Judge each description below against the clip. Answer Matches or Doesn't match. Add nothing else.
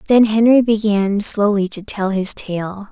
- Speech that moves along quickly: Doesn't match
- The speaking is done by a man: Doesn't match